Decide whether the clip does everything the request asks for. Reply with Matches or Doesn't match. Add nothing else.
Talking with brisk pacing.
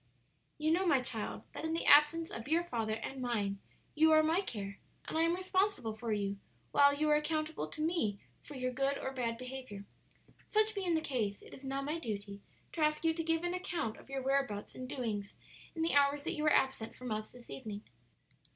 Matches